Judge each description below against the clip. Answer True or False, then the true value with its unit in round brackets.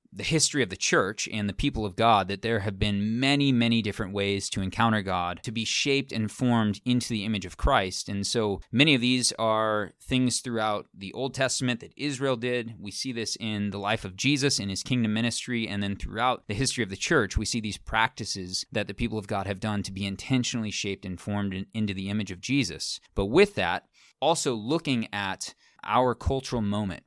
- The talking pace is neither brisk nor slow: False (215 wpm)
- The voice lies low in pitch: True (110 Hz)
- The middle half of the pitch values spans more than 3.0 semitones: True (3.7 semitones)